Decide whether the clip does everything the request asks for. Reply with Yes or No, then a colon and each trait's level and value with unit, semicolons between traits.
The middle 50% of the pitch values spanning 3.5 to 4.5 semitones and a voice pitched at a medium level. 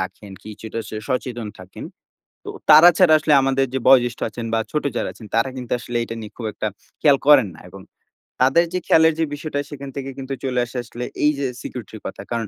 No: average, 3.8 semitones; low, 130 Hz